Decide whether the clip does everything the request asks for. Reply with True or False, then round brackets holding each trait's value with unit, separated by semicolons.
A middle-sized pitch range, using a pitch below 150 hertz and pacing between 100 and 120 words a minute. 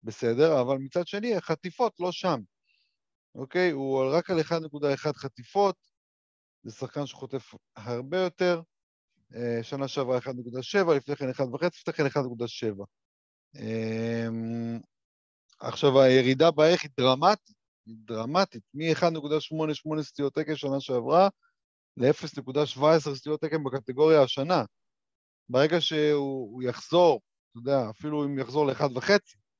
True (4.7 semitones; 140 Hz; 115 wpm)